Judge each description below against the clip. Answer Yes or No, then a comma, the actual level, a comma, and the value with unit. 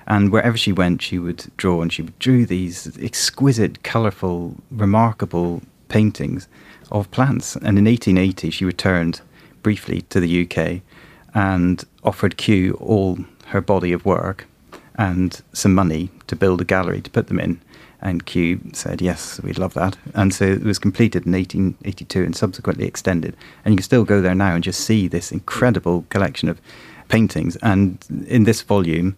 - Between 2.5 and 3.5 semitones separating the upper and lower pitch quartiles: Yes, average, 3.0 semitones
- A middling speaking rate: Yes, average, 165 wpm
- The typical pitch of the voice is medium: No, very low, 95 Hz